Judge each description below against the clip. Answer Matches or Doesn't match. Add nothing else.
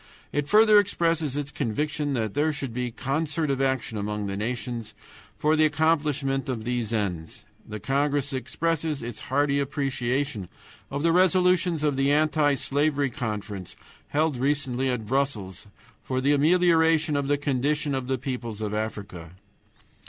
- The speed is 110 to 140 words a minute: Doesn't match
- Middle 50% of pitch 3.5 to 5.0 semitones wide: Matches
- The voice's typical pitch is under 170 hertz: Matches